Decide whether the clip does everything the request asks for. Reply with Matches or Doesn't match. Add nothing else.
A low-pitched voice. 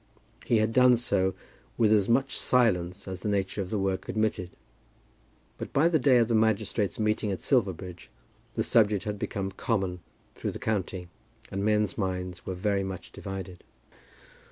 Matches